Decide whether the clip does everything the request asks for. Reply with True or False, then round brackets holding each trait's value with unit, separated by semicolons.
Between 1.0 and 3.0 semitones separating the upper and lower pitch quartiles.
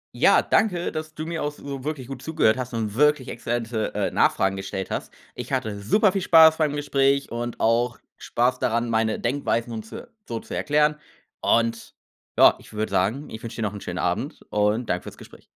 False (4.8 semitones)